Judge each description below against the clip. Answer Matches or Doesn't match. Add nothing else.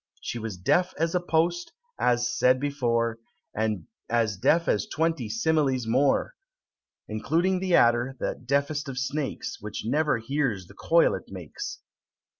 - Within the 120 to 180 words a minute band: Matches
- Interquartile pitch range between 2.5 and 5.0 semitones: Doesn't match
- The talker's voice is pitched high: Doesn't match